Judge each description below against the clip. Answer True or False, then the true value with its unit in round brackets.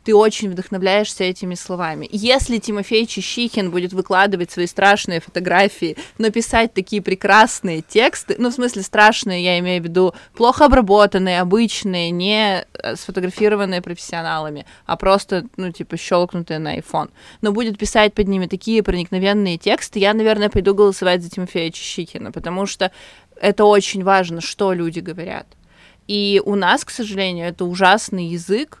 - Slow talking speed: False (145 wpm)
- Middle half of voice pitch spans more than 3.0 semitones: False (2.7 semitones)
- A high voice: True (195 Hz)